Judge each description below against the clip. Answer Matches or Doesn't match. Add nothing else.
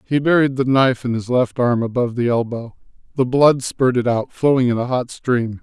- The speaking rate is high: Matches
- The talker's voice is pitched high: Doesn't match